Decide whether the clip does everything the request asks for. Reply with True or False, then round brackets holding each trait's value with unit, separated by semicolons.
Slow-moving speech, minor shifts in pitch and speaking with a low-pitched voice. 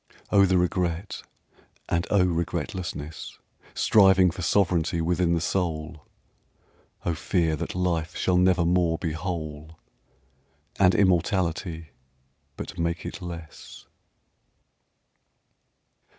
True (100 wpm; 1.9 semitones; 85 Hz)